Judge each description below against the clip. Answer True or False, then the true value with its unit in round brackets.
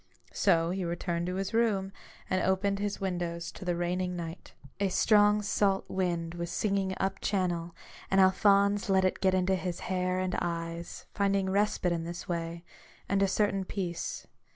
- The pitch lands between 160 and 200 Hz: True (185 Hz)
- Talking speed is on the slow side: False (170 wpm)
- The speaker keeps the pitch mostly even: True (2.3 semitones)